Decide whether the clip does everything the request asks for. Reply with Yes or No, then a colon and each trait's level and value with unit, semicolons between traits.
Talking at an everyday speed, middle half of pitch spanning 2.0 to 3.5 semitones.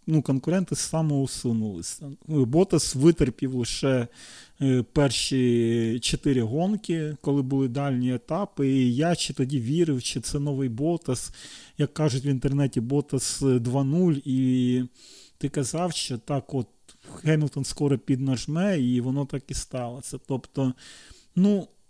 Yes: average, 120 wpm; average, 3.2 semitones